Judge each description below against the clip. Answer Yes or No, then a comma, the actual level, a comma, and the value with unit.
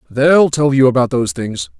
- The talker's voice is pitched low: Yes, low, 130 Hz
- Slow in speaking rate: No, average, 200 wpm